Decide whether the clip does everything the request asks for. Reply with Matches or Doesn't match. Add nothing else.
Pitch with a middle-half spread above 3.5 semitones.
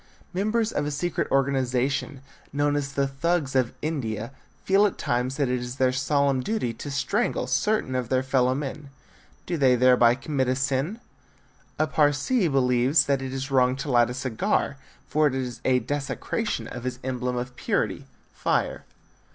Doesn't match